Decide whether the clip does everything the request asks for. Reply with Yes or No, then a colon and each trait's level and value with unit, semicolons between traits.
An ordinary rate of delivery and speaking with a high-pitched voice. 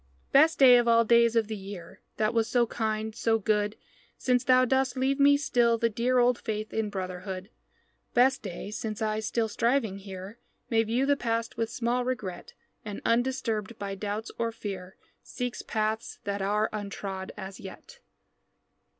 Yes: average, 165 wpm; high, 225 Hz